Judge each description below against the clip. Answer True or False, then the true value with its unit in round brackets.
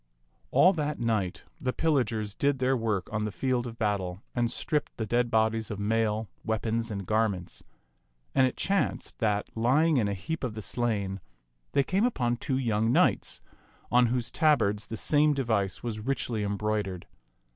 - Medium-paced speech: True (170 wpm)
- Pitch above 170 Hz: False (115 Hz)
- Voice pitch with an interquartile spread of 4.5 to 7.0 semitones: False (3.6 semitones)